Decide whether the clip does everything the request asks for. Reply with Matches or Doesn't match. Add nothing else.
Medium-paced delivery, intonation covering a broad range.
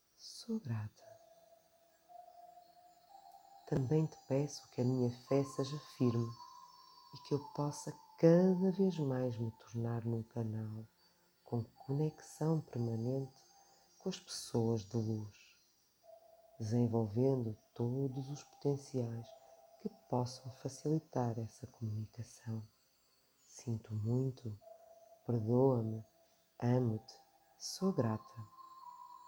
Doesn't match